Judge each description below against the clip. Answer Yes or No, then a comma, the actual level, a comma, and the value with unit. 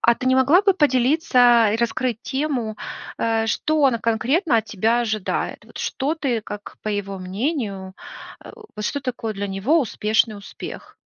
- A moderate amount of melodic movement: Yes, average, 4.1 semitones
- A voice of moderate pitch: No, high, 235 Hz